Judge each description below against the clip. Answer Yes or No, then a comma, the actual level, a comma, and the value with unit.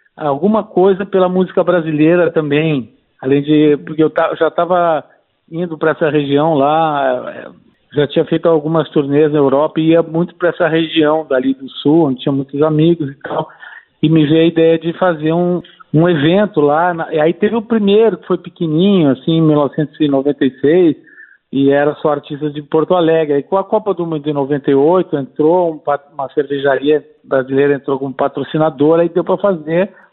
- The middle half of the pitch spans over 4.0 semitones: No, average, 3.0 semitones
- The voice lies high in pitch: No, medium, 160 Hz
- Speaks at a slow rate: No, fast, 185 wpm